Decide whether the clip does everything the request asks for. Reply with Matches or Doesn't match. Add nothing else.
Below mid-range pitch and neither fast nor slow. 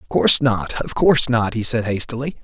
Matches